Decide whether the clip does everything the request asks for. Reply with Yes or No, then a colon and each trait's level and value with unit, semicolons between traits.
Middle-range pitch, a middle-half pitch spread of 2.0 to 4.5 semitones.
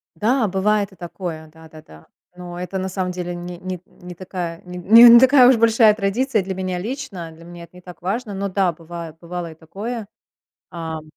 Yes: medium, 180 Hz; average, 3.5 semitones